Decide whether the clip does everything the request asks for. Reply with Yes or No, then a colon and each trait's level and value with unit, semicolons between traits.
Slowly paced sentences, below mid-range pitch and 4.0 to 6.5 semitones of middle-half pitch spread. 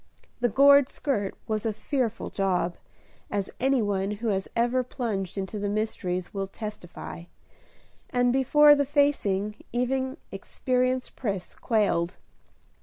No: slow, 125 wpm; high, 225 Hz; average, 4.7 semitones